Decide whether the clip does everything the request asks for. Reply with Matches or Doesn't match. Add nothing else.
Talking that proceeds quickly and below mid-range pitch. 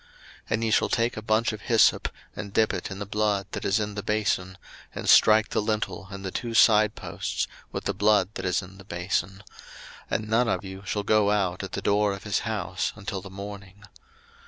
Matches